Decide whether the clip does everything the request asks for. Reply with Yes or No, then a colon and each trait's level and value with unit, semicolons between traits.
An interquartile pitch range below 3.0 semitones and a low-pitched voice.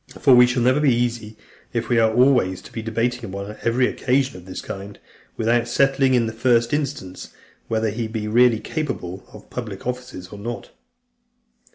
Yes: narrow, 2.6 semitones; low, 115 Hz